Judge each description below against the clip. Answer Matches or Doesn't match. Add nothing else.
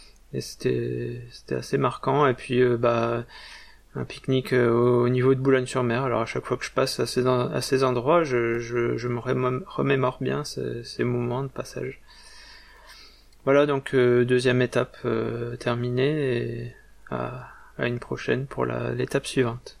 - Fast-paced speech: Doesn't match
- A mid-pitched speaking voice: Doesn't match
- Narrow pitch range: Matches